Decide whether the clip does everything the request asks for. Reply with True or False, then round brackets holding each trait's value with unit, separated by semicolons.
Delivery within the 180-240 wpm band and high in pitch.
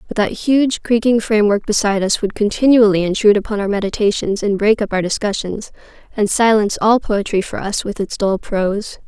True (185 wpm; 210 Hz)